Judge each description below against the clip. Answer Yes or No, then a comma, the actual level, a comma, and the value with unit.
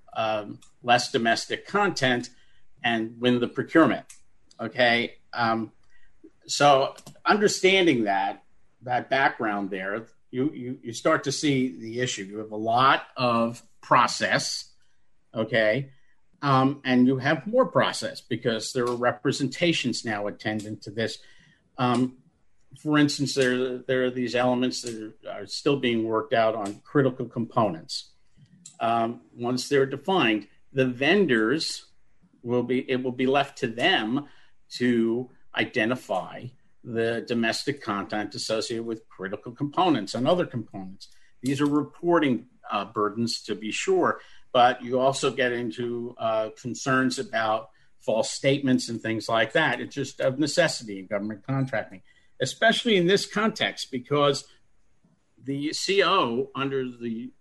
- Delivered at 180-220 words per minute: No, slow, 135 wpm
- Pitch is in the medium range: No, low, 125 Hz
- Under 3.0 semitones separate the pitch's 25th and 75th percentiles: No, average, 3.3 semitones